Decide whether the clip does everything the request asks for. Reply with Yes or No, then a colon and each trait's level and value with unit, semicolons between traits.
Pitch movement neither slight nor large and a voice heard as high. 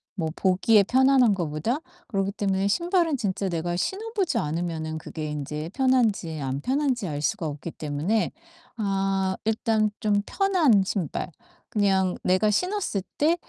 No: wide, 6.7 semitones; high, 200 Hz